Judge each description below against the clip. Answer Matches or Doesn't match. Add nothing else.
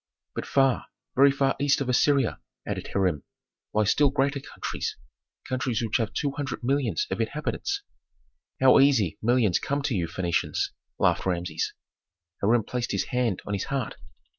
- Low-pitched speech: Matches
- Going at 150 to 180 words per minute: Matches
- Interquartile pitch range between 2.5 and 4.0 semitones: Doesn't match